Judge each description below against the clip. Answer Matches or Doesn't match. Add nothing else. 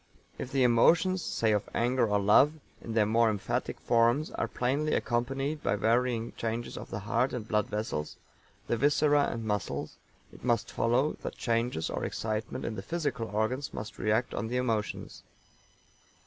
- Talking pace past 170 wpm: Doesn't match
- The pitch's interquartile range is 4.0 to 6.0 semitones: Doesn't match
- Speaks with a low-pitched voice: Matches